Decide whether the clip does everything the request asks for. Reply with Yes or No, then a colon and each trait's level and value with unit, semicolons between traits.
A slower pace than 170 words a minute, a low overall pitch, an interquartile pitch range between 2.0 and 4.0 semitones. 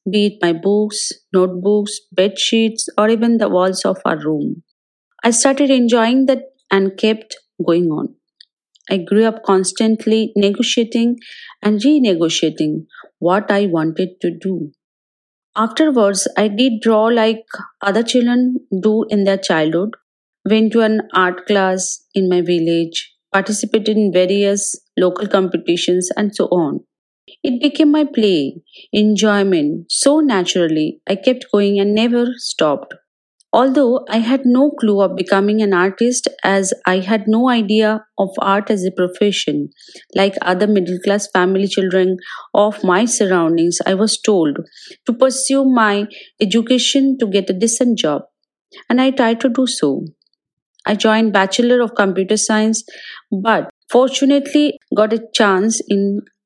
No: average, 140 wpm; high, 210 Hz; average, 3.6 semitones